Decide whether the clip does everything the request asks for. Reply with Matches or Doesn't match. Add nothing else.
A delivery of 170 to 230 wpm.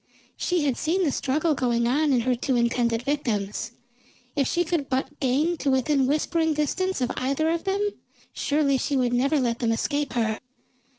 Matches